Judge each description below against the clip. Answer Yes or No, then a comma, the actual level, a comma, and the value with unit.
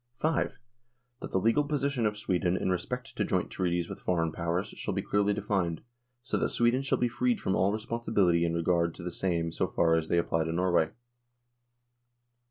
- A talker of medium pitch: No, very low, 95 Hz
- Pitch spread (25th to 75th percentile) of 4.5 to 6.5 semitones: Yes, average, 4.8 semitones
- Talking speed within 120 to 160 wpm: No, average, 190 wpm